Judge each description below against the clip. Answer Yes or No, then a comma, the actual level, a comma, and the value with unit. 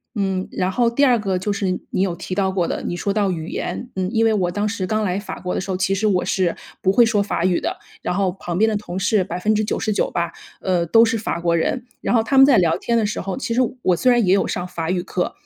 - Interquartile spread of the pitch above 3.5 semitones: No, average, 3.1 semitones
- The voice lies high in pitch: Yes, high, 195 Hz